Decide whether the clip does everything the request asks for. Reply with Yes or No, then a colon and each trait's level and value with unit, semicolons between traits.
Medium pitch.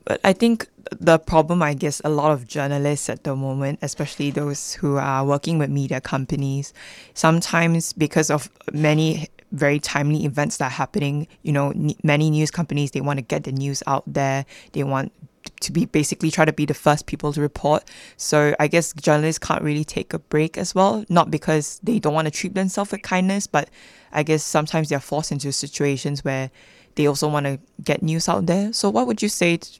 Yes: medium, 150 Hz